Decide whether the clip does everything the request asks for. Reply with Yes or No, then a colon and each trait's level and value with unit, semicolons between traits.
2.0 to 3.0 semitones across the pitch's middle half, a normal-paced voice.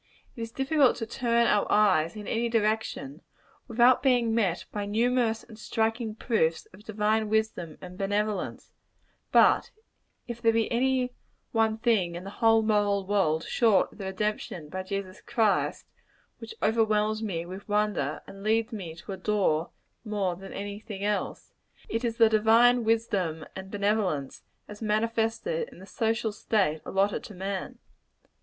Yes: narrow, 2.6 semitones; average, 155 wpm